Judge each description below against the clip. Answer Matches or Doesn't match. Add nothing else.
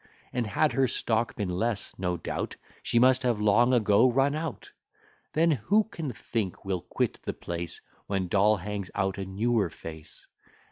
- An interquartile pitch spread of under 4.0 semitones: Doesn't match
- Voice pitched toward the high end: Doesn't match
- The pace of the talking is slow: Doesn't match